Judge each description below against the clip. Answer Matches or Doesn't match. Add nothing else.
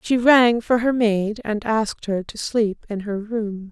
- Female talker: Matches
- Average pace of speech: Doesn't match